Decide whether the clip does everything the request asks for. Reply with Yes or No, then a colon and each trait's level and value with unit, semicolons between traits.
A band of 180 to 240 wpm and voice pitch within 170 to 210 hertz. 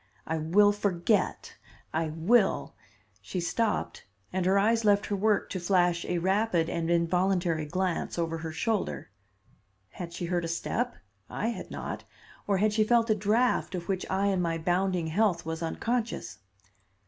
No: average, 165 wpm; medium, 185 Hz